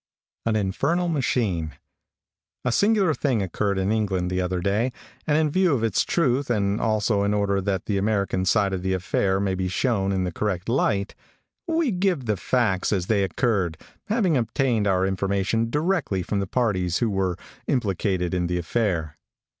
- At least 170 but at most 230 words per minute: Yes, average, 175 wpm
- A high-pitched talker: No, low, 100 Hz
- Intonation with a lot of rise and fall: No, average, 4.7 semitones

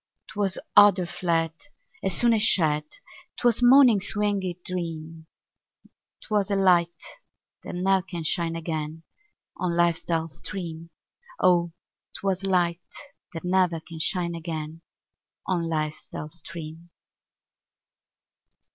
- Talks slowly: Yes, slow, 110 wpm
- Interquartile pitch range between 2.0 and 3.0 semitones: Yes, average, 2.7 semitones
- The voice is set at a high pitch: No, medium, 170 Hz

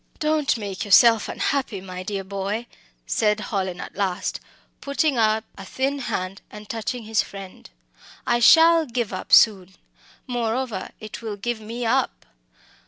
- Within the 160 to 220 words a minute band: No, average, 145 wpm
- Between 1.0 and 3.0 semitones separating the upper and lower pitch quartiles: No, average, 3.7 semitones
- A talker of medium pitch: No, high, 220 Hz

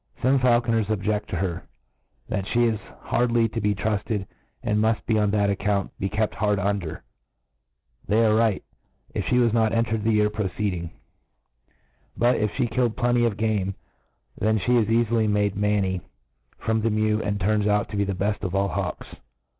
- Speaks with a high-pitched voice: No, low, 105 Hz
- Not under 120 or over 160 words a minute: No, average, 185 wpm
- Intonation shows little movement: Yes, narrow, 1.9 semitones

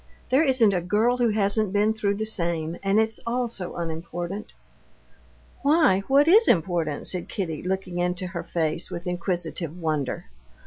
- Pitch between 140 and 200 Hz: Yes, high, 190 Hz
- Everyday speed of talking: Yes, average, 160 wpm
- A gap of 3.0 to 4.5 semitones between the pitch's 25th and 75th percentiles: Yes, average, 4.2 semitones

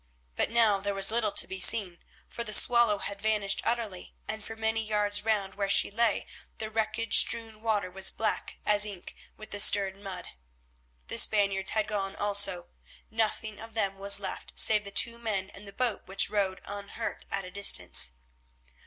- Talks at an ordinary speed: Yes, average, 180 wpm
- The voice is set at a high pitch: Yes, high, 205 Hz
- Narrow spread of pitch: Yes, narrow, 2.0 semitones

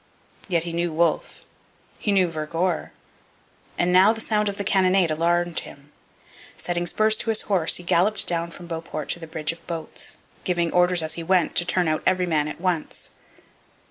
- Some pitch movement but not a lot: No, narrow, 2.1 semitones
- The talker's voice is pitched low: No, medium, 175 Hz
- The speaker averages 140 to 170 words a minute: No, average, 185 wpm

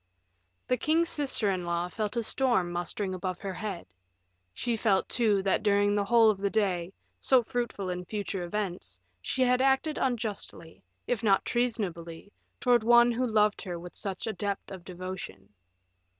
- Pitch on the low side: No, high, 205 Hz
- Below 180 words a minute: Yes, average, 165 wpm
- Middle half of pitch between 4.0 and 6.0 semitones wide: Yes, average, 4.6 semitones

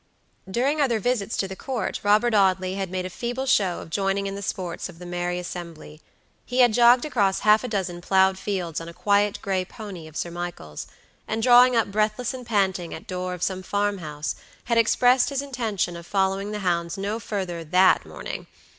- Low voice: No, high, 195 Hz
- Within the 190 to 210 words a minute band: Yes, fast, 205 wpm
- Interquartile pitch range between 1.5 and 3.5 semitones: No, average, 3.9 semitones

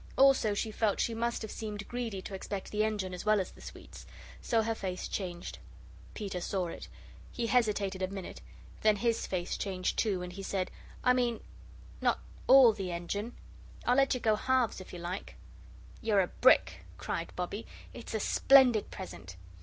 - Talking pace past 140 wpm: Yes, average, 180 wpm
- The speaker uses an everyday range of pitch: Yes, average, 3.6 semitones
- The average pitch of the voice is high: Yes, high, 210 Hz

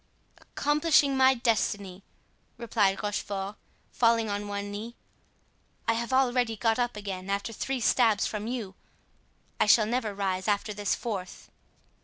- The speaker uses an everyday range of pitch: Yes, average, 3.0 semitones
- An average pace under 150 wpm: Yes, slow, 135 wpm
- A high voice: Yes, high, 215 Hz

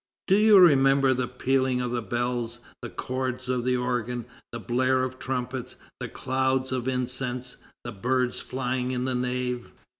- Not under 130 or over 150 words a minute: No, average, 160 wpm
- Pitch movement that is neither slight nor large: No, narrow, 1.0 semitones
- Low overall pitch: Yes, low, 125 Hz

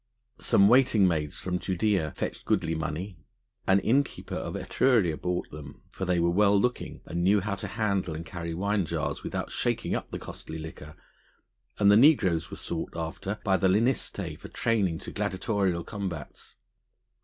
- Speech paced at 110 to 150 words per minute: No, average, 165 wpm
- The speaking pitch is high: No, very low, 95 Hz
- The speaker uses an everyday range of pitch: Yes, average, 3.7 semitones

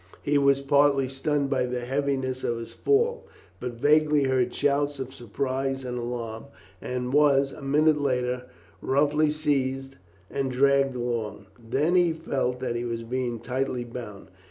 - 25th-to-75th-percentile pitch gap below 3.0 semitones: Yes, narrow, 2.4 semitones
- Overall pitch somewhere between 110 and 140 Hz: Yes, low, 135 Hz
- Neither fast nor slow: Yes, average, 155 wpm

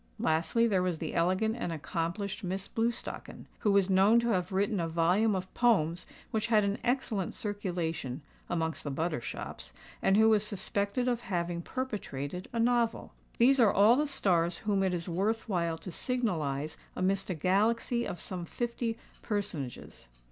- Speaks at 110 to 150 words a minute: No, average, 165 wpm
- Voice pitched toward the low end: No, high, 195 Hz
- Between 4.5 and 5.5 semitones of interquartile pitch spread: Yes, average, 4.8 semitones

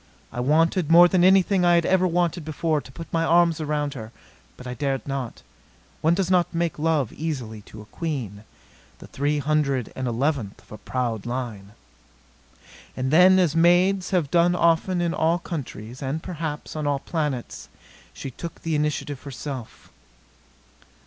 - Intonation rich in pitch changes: No, average, 4.6 semitones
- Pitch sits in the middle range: Yes, medium, 155 Hz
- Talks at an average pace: Yes, average, 165 wpm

